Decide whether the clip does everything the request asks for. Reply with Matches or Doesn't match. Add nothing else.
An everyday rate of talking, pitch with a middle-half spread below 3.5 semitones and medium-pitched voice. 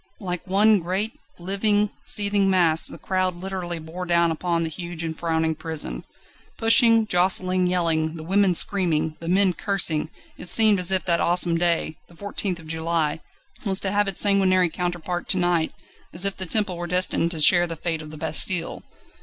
Matches